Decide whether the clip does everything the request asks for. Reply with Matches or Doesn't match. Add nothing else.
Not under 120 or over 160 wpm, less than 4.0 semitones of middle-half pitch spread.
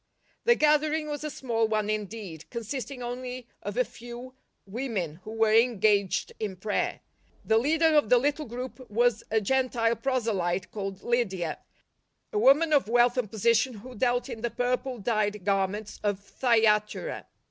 Matches